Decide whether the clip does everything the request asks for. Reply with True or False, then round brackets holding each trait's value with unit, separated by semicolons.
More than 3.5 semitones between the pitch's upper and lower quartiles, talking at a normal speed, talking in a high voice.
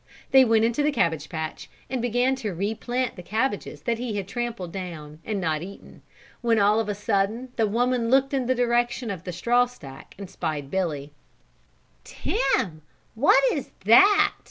True (5.3 semitones; 180 wpm; 220 Hz)